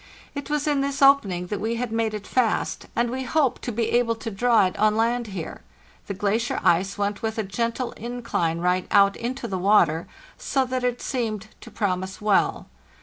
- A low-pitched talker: No, high, 225 Hz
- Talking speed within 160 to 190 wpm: No, average, 200 wpm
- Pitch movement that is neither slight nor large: Yes, average, 3.6 semitones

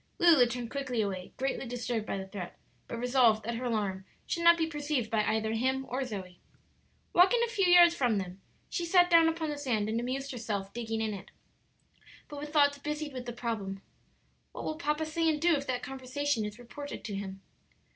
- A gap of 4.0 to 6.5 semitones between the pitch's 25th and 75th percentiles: Yes, wide, 5.4 semitones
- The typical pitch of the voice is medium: No, very high, 250 Hz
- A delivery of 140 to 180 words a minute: No, fast, 205 wpm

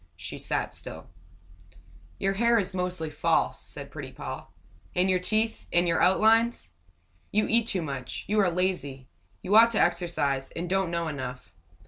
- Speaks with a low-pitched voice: No, medium, 180 Hz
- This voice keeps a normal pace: Yes, average, 160 wpm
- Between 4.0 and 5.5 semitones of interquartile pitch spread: Yes, average, 4.6 semitones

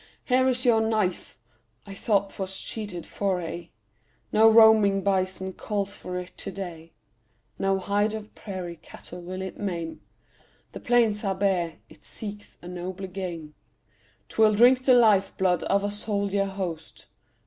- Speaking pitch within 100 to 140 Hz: No, high, 195 Hz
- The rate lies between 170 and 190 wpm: No, average, 150 wpm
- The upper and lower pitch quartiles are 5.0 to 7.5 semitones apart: No, average, 2.7 semitones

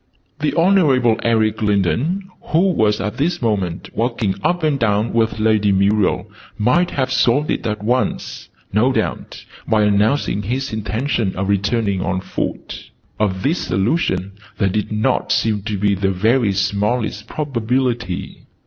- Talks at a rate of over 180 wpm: No, average, 145 wpm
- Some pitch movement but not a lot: Yes, average, 4.2 semitones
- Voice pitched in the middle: No, low, 110 Hz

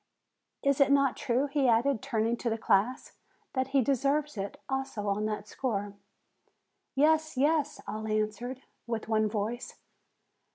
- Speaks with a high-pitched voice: Yes, high, 245 Hz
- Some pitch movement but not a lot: Yes, average, 4.3 semitones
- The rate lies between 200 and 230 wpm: No, average, 150 wpm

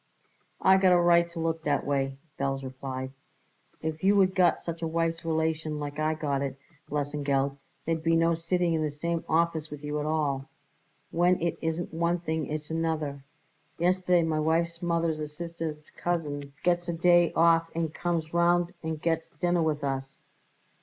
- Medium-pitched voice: Yes, medium, 160 Hz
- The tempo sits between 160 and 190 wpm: Yes, average, 175 wpm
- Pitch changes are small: Yes, narrow, 2.3 semitones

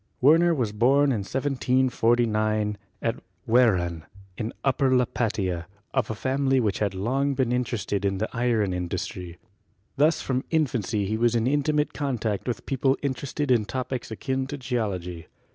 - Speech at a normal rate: Yes, average, 155 wpm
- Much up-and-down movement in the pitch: No, average, 4.2 semitones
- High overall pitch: No, low, 120 Hz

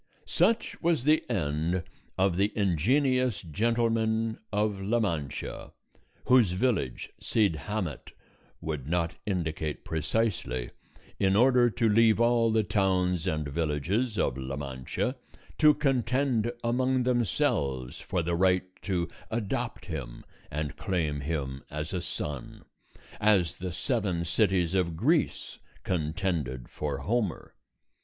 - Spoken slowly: Yes, slow, 120 wpm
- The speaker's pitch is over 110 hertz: No, very low, 95 Hz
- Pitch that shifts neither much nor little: No, wide, 6.6 semitones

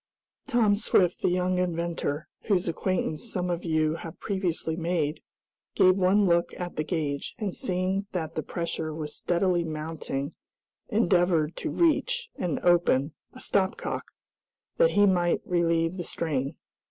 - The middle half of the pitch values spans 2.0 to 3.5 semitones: Yes, average, 2.7 semitones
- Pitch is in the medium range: Yes, medium, 175 Hz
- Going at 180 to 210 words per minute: No, average, 145 wpm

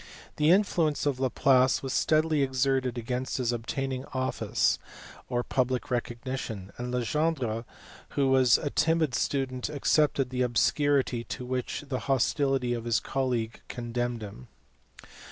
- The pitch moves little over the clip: Yes, narrow, 2.3 semitones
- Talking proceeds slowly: Yes, slow, 130 wpm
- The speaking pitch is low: Yes, low, 130 Hz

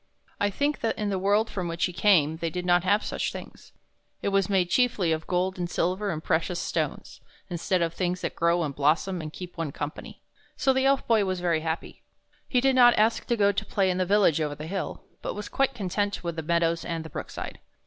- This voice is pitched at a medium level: Yes, medium, 180 Hz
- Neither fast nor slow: No, fast, 235 wpm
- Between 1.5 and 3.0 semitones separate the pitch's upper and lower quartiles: No, average, 3.5 semitones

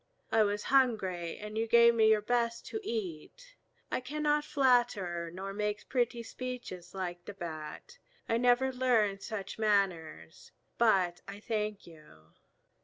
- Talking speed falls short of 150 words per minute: Yes, average, 140 wpm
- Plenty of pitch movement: No, average, 4.8 semitones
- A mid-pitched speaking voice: No, high, 215 Hz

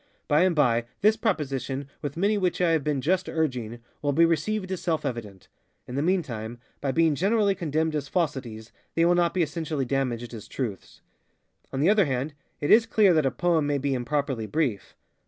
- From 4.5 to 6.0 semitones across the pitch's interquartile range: Yes, average, 4.9 semitones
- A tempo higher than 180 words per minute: Yes, average, 195 wpm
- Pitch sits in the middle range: Yes, medium, 150 Hz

